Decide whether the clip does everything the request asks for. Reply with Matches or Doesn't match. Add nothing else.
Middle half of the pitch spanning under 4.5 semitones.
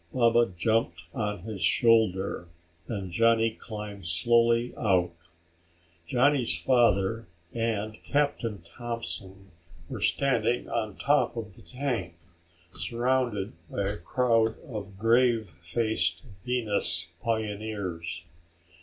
Matches